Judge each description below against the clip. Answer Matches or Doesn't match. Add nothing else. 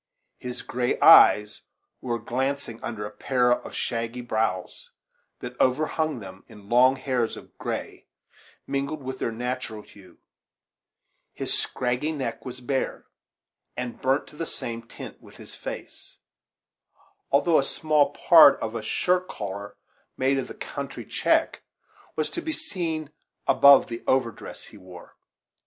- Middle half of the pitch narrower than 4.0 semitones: Matches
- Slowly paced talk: Doesn't match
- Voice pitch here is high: Doesn't match